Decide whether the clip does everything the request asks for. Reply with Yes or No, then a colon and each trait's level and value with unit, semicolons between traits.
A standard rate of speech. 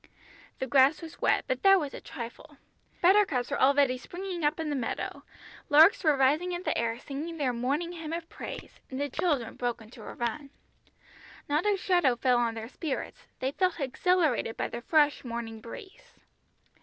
Yes: average, 180 wpm